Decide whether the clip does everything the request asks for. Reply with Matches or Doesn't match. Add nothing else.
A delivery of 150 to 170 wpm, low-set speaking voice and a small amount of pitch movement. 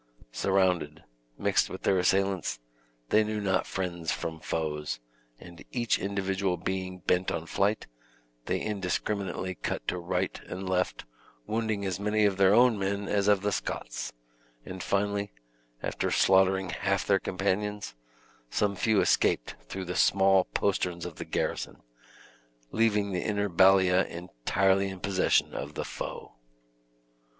Doesn't match